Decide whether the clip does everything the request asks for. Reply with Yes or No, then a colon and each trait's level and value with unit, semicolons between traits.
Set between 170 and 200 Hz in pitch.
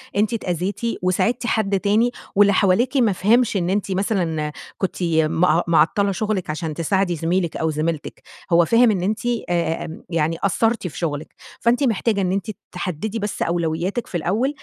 Yes: high, 190 Hz